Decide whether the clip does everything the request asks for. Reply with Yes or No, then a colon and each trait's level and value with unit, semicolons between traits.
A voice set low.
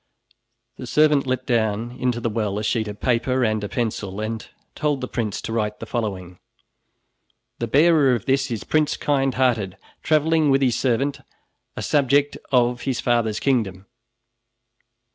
Yes: low, 120 Hz